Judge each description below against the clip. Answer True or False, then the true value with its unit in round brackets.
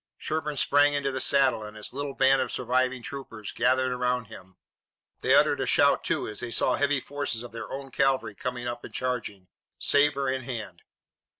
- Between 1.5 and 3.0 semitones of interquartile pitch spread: True (2.6 semitones)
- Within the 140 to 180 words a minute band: False (190 wpm)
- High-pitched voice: False (130 Hz)